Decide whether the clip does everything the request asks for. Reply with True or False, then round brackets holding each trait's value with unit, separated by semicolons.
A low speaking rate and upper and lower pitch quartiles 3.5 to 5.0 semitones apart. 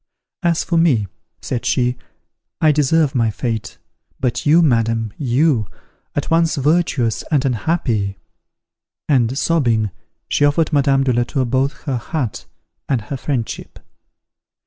True (130 wpm; 4.4 semitones)